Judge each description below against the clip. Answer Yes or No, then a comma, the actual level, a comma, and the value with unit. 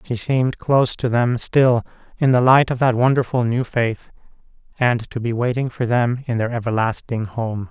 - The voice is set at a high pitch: No, low, 120 Hz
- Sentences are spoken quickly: No, average, 185 wpm